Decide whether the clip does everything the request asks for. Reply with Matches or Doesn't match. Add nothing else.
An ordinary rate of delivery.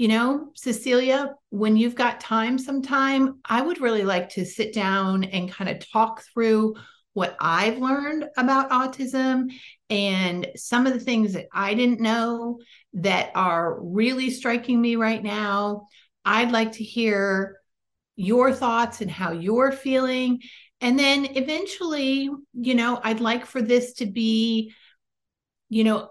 Matches